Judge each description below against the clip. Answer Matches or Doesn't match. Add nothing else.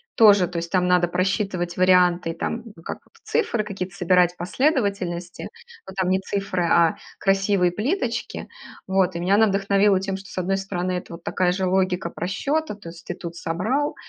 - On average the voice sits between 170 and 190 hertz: Matches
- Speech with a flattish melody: Matches